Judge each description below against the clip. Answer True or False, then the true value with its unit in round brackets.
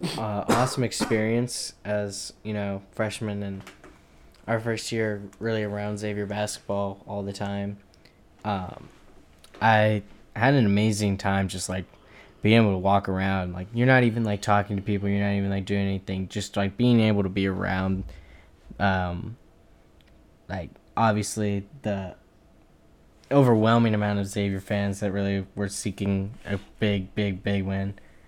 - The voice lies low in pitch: True (100 Hz)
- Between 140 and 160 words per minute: True (150 wpm)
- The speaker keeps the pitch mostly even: True (1.7 semitones)